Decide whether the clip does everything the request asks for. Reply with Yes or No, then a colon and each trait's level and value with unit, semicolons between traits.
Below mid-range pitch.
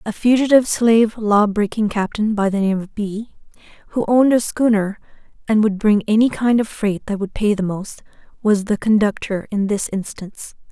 No: high, 210 Hz